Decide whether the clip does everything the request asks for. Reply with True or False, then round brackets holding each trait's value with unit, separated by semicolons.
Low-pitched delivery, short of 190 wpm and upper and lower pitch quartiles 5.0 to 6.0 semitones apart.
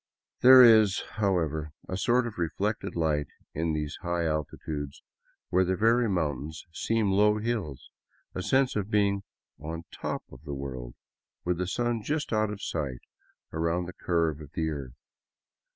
True (85 Hz; 155 wpm; 5.5 semitones)